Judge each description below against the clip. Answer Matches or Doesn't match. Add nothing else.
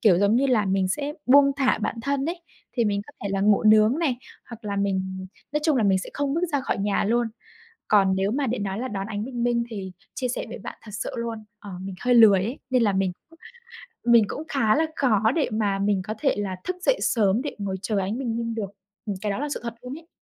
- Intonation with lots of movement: Doesn't match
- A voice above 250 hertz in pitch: Doesn't match